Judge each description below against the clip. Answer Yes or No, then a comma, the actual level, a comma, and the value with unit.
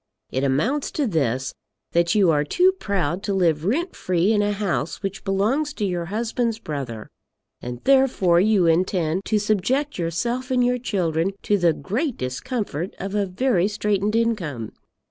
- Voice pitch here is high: Yes, high, 195 Hz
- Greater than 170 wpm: No, average, 165 wpm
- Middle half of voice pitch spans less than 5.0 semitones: No, wide, 5.5 semitones